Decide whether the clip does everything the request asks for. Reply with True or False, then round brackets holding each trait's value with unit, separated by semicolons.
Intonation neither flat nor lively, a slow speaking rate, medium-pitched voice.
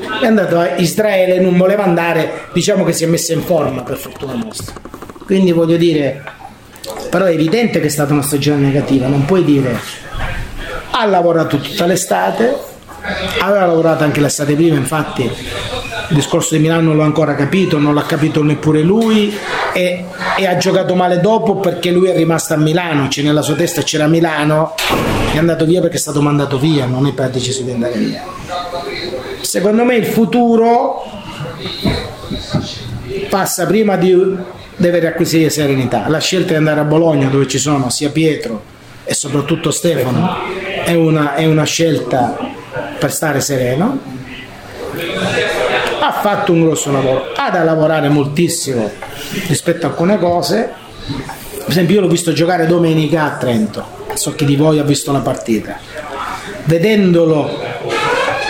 False (3.7 semitones; 155 wpm; 160 Hz)